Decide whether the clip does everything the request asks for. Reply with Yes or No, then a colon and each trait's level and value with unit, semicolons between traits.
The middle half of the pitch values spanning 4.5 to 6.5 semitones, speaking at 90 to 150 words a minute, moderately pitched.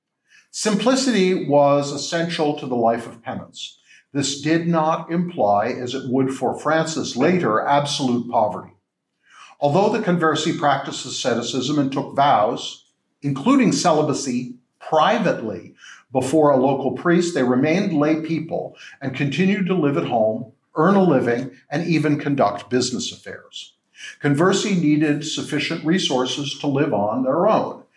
No: average, 4.0 semitones; slow, 135 wpm; medium, 145 Hz